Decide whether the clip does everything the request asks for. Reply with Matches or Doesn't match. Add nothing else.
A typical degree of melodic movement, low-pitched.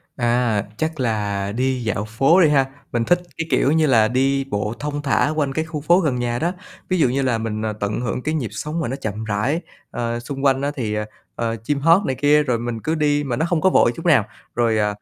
Matches